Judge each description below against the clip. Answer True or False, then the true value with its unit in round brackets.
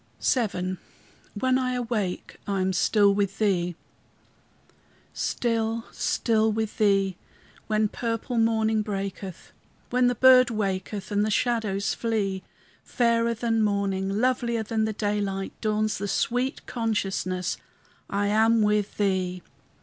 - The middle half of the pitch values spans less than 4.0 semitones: True (2.7 semitones)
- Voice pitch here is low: False (215 Hz)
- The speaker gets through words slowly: True (120 wpm)